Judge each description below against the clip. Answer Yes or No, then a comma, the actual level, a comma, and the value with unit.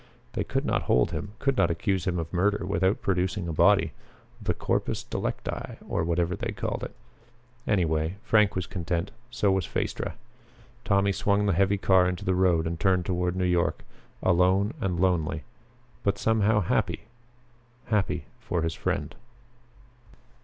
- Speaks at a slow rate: No, average, 155 wpm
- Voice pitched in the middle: No, very low, 90 Hz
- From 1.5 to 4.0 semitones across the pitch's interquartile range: Yes, narrow, 2.6 semitones